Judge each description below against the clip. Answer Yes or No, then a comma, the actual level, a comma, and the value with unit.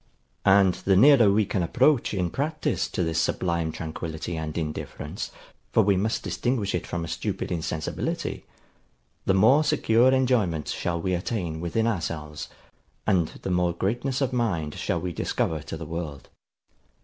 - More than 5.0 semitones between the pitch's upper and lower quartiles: Yes, wide, 5.5 semitones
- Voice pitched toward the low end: Yes, very low, 90 Hz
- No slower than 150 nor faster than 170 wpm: Yes, average, 155 wpm